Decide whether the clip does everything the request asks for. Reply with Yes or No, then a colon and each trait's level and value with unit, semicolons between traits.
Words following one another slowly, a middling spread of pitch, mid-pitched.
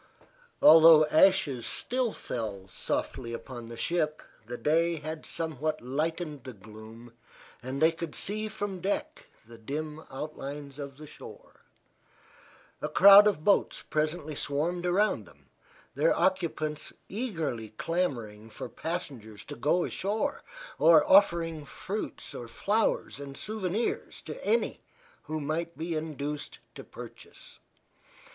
Yes: slow, 125 wpm; average, 4.7 semitones; medium, 155 Hz